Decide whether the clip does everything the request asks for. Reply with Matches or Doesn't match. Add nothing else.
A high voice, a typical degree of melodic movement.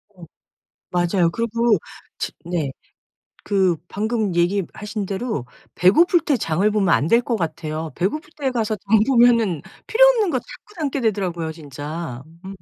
Doesn't match